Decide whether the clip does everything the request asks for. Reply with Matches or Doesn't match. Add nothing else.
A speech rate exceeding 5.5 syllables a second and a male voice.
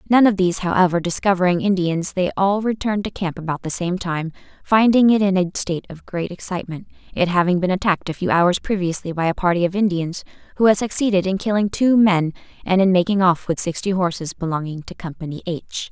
Doesn't match